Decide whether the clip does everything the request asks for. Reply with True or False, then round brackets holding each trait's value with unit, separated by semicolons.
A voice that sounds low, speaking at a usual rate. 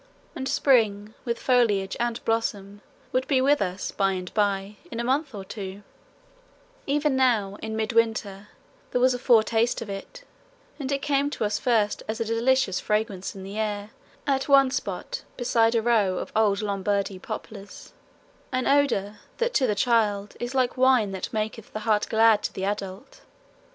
False (220 Hz; 170 wpm)